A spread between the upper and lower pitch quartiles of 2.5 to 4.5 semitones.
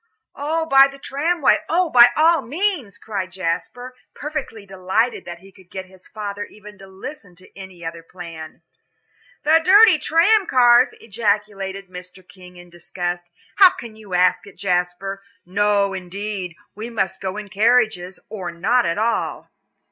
No: average, 5.2 semitones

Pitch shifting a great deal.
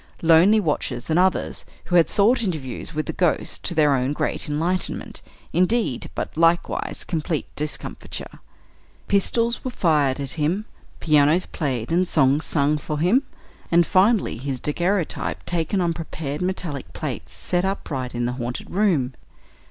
No: average, 4.4 semitones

